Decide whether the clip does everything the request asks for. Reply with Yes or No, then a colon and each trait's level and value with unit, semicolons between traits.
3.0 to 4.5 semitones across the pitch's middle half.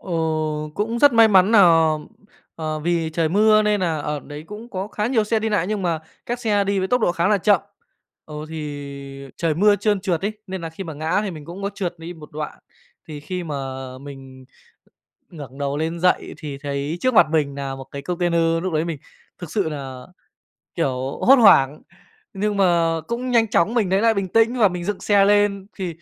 No: wide, 5.4 semitones